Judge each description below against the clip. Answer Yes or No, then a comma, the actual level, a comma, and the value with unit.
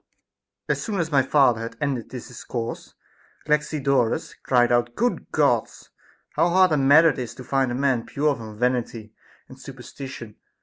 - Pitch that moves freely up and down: No, average, 3.4 semitones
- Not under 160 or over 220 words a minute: Yes, average, 175 wpm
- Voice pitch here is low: Yes, low, 130 Hz